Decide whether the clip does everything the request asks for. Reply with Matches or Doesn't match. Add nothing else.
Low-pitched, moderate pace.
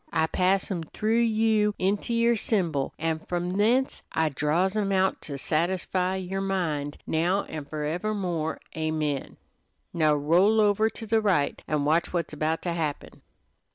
Doesn't match